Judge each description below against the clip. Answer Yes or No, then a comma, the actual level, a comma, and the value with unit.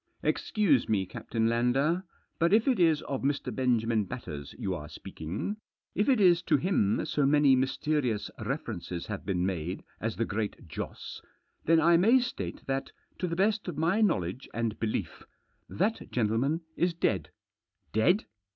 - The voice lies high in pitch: No, low, 135 Hz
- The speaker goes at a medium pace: Yes, average, 160 wpm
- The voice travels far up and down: Yes, wide, 8.0 semitones